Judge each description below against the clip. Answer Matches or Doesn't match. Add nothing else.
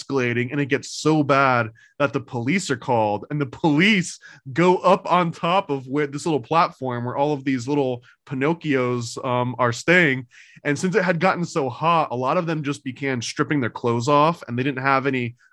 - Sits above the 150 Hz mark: Doesn't match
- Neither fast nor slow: Doesn't match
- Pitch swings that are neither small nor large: Matches